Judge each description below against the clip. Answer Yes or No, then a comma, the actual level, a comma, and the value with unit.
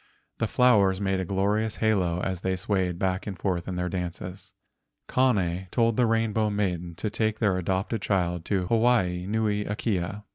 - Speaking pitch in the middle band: No, very low, 95 Hz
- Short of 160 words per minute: No, average, 170 wpm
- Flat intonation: No, average, 3.2 semitones